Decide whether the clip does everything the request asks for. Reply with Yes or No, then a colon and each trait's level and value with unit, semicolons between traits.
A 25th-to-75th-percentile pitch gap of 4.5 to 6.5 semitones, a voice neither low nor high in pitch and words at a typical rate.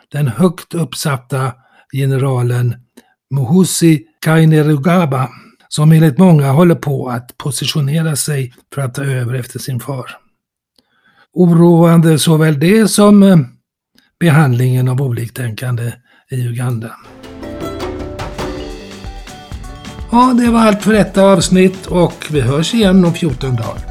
No: average, 5.1 semitones; medium, 150 Hz; slow, 110 wpm